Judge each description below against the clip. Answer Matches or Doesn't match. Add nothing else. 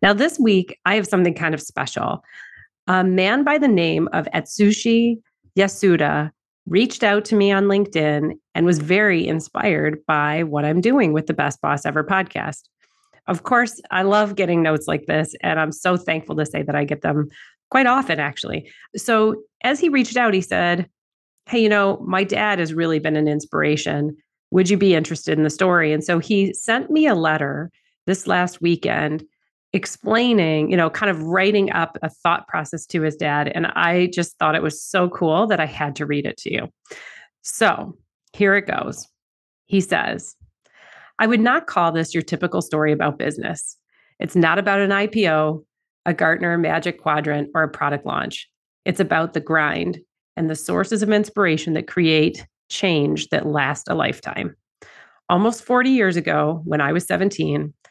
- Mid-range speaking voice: Matches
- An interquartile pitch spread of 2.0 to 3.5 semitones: Doesn't match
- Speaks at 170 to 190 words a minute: Matches